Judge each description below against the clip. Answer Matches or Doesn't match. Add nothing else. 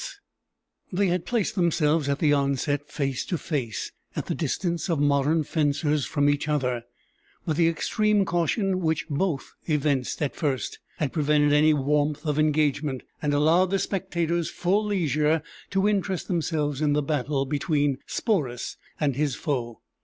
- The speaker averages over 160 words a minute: Doesn't match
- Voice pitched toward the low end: Doesn't match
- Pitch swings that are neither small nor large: Matches